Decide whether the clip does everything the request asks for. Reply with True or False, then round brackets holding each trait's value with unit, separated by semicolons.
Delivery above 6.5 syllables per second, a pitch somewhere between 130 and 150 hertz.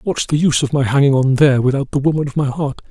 True (6.9 syllables/s; 140 Hz)